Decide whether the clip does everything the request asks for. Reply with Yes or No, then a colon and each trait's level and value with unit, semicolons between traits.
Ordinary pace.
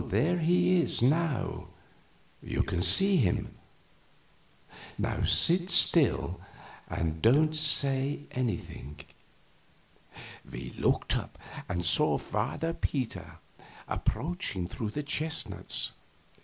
No: slow, 90 wpm